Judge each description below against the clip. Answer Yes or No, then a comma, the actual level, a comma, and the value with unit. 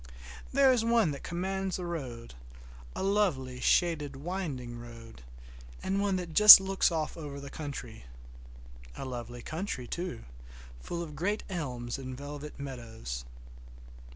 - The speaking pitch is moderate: Yes, medium, 150 Hz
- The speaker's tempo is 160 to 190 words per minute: No, slow, 135 wpm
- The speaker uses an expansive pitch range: Yes, wide, 6.8 semitones